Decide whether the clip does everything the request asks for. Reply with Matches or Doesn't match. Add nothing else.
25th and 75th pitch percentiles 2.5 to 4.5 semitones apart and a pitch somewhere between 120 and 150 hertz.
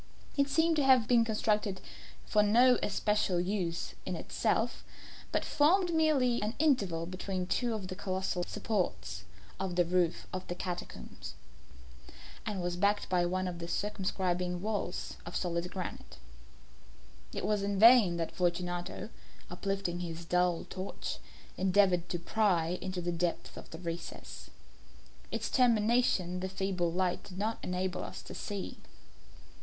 Doesn't match